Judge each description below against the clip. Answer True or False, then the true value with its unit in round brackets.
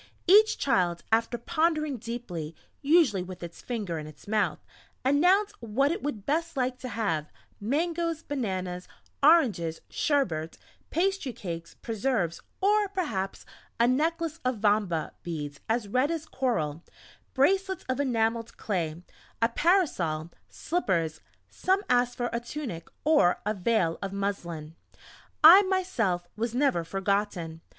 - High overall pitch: True (230 Hz)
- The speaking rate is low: True (130 wpm)